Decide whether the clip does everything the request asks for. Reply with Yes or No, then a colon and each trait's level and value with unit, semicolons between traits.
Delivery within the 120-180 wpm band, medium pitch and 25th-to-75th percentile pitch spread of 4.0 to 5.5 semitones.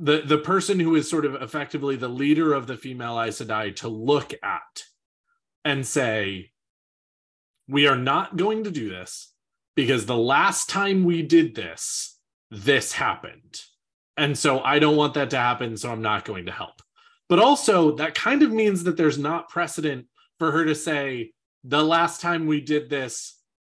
Yes: average, 175 wpm; medium, 150 Hz; average, 4.5 semitones